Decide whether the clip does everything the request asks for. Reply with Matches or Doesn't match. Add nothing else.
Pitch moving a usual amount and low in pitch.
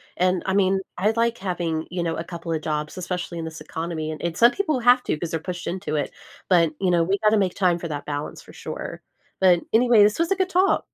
Doesn't match